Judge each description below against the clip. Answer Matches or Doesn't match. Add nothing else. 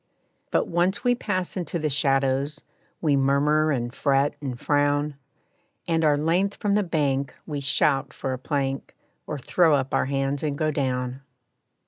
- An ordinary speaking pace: Matches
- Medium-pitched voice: Matches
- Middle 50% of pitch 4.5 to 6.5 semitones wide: Doesn't match